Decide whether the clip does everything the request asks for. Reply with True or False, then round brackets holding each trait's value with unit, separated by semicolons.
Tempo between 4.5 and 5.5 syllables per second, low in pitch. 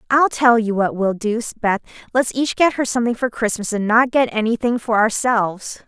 False (5.3 syllables/s; 230 Hz)